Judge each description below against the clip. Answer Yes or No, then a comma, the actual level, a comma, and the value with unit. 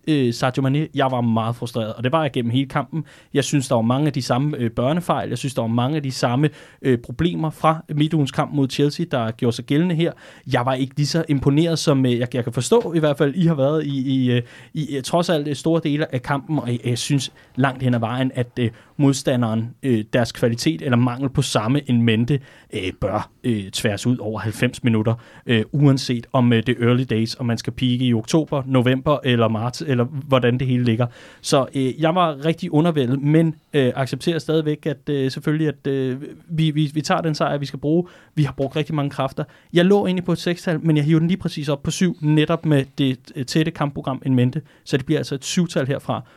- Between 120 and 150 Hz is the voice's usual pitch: Yes, medium, 140 Hz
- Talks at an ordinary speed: No, fast, 230 wpm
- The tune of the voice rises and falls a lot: No, average, 3.8 semitones